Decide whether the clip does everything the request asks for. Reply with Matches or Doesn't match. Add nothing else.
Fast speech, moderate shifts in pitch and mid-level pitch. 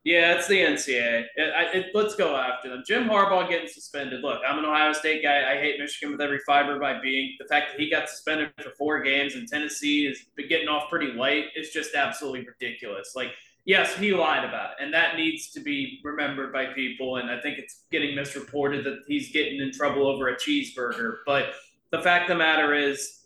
Matches